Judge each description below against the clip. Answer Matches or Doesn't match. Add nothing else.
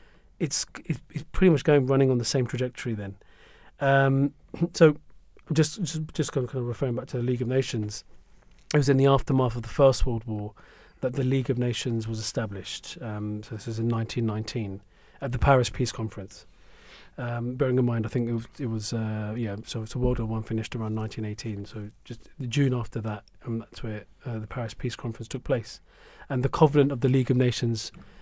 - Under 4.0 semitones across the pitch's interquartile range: Matches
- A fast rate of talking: Matches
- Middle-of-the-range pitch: Doesn't match